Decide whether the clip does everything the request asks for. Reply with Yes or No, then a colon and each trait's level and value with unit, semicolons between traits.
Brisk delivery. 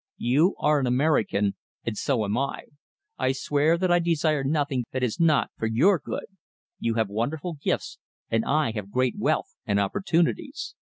No: average, 170 wpm